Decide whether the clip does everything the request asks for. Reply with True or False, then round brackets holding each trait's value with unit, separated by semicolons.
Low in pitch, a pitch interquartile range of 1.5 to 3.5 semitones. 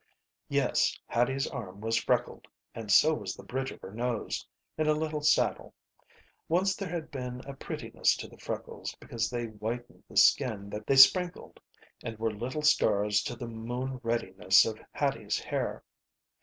False (120 Hz; 4.0 semitones)